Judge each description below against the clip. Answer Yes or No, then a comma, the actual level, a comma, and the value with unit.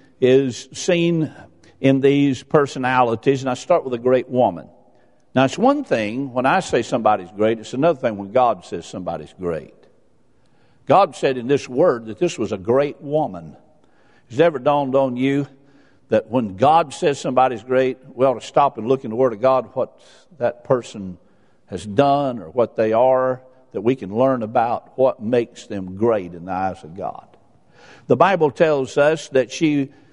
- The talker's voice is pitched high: No, low, 130 Hz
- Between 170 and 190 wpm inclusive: Yes, average, 180 wpm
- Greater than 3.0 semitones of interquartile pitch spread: No, narrow, 2.6 semitones